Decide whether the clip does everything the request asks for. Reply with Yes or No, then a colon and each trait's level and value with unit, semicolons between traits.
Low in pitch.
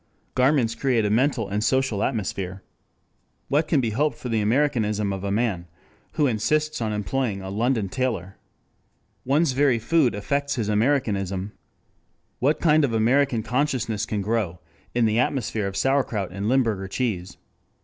Yes: low, 115 Hz